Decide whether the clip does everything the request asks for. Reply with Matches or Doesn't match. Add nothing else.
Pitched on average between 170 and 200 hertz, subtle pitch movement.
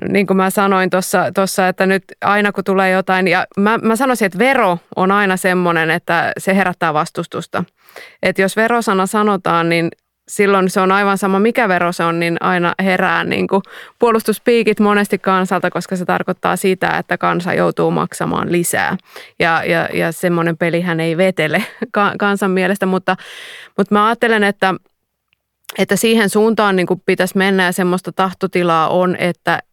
Matches